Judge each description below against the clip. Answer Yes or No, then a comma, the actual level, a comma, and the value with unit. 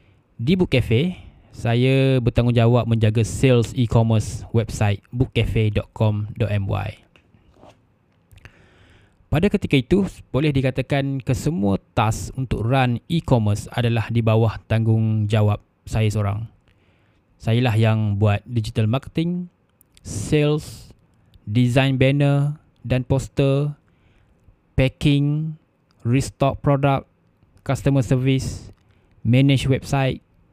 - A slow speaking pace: Yes, slow, 85 wpm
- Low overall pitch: Yes, low, 115 Hz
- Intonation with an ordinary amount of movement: Yes, average, 4.1 semitones